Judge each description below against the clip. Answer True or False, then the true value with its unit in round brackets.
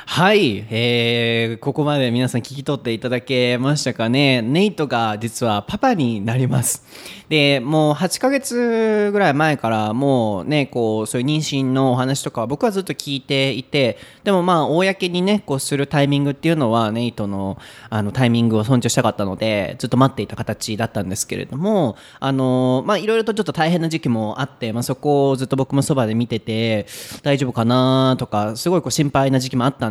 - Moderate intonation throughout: True (4.3 semitones)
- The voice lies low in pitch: True (130 Hz)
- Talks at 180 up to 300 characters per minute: False (375 characters per minute)